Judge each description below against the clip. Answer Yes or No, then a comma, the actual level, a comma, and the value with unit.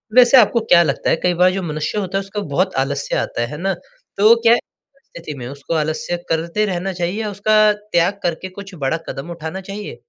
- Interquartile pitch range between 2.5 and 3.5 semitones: No, average, 4.5 semitones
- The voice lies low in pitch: No, medium, 185 Hz